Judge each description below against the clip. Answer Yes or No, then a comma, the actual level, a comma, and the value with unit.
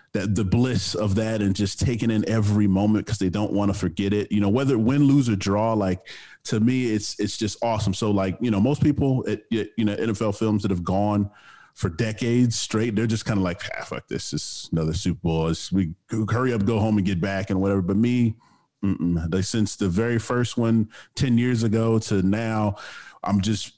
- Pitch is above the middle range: No, low, 105 Hz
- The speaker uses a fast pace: Yes, fast, 225 wpm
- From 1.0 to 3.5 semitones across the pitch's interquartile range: Yes, narrow, 2.5 semitones